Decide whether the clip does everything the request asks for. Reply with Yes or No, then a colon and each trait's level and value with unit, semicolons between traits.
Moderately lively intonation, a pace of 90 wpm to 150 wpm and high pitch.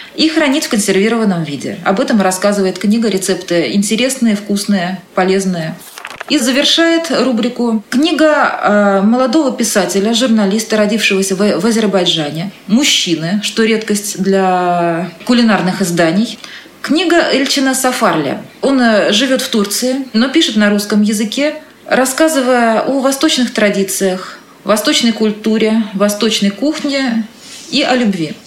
Yes: average, 4.8 semitones; slow, 110 wpm; high, 220 Hz